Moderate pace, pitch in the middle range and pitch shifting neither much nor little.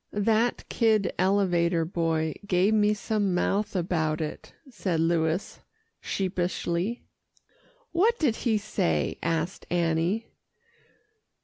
No: slow, 100 wpm; medium, 180 Hz; average, 4.2 semitones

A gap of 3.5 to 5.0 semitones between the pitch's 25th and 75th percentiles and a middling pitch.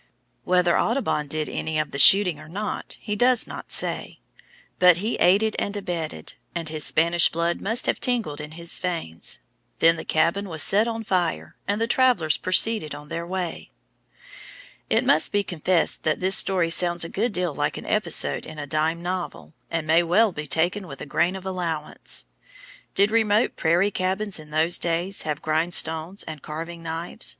Yes: average, 3.9 semitones; medium, 175 Hz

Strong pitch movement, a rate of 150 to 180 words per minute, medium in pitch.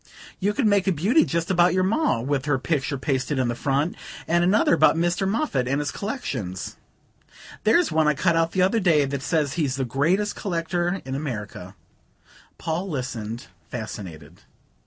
Yes: wide, 5.9 semitones; average, 175 wpm; medium, 155 Hz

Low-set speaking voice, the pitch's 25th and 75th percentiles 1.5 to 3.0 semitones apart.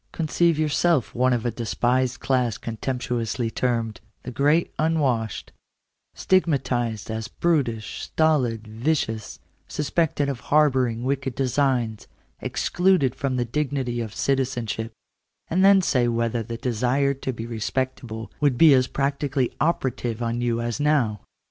No: low, 125 Hz; average, 3.6 semitones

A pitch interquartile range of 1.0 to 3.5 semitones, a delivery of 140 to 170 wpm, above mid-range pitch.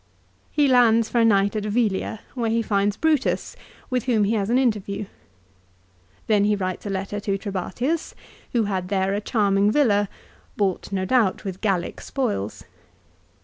Yes: average, 2.9 semitones; average, 160 wpm; high, 205 Hz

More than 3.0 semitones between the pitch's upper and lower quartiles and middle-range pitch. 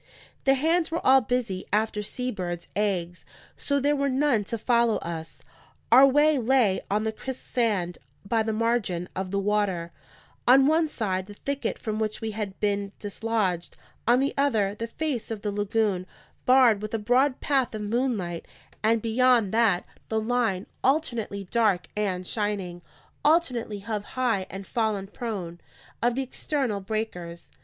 No: average, 4.1 semitones; high, 220 Hz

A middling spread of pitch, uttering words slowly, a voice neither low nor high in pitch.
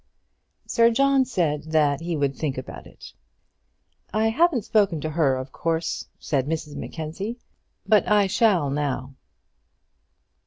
No: wide, 6.7 semitones; slow, 130 wpm; medium, 165 Hz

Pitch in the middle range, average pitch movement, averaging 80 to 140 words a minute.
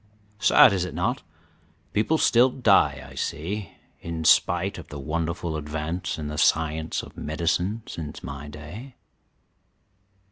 No: very low, 85 Hz; average, 4.3 semitones; slow, 135 wpm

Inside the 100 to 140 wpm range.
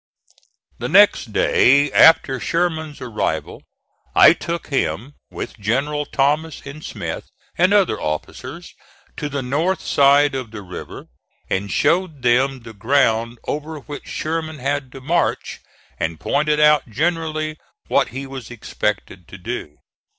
Yes: slow, 135 wpm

